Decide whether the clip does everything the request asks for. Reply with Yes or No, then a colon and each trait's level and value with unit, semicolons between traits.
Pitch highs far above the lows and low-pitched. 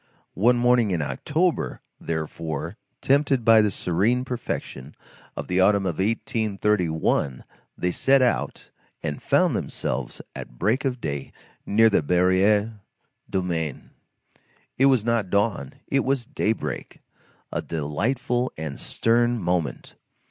Yes: wide, 6.2 semitones; low, 105 Hz